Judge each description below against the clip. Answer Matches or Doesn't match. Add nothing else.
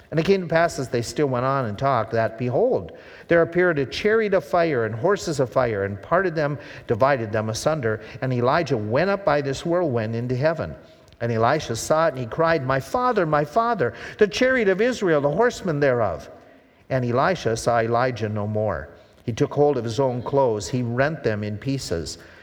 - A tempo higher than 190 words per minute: Matches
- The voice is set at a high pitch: Doesn't match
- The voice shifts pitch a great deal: Matches